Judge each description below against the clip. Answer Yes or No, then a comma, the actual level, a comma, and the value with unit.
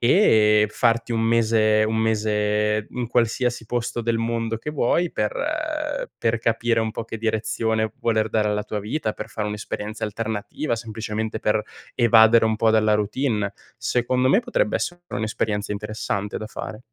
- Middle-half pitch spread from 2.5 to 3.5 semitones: No, narrow, 1.7 semitones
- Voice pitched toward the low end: Yes, low, 110 Hz